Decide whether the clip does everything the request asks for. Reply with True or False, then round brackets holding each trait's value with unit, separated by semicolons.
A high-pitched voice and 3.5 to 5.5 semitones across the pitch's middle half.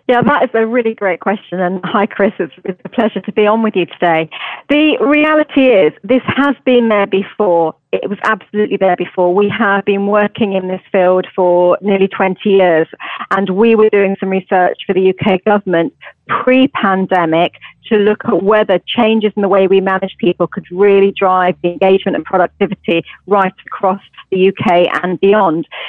False (195 Hz; 2.4 semitones)